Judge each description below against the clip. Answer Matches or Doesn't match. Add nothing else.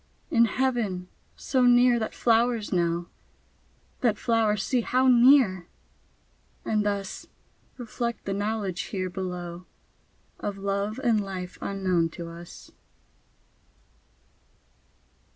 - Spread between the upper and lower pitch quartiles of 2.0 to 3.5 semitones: Doesn't match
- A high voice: Matches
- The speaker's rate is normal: Doesn't match